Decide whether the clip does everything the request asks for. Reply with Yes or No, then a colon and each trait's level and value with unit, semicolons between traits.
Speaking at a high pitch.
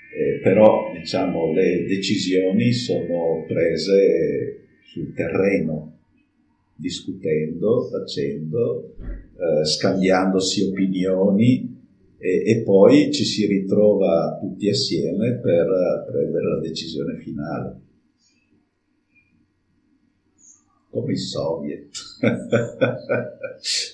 No: low, 105 Hz